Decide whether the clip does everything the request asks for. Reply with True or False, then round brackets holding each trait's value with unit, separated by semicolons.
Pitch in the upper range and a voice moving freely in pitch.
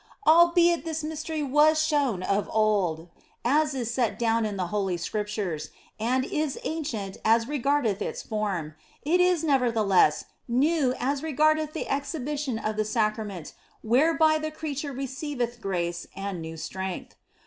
True (250 Hz; 6.5 semitones)